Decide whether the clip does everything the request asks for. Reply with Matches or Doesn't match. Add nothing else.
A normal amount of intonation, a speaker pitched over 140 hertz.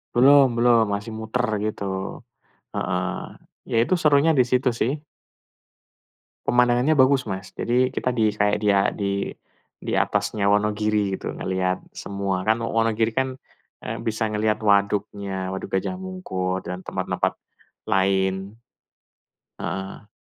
Doesn't match